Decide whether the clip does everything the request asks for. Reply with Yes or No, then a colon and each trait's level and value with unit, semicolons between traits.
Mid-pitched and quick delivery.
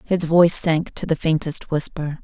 No: medium, 160 Hz; average, 190 wpm